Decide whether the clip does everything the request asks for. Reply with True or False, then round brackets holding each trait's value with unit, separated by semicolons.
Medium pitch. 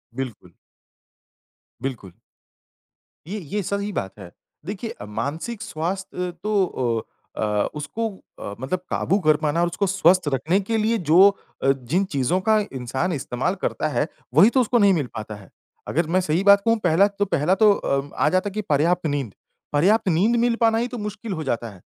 True (180 Hz)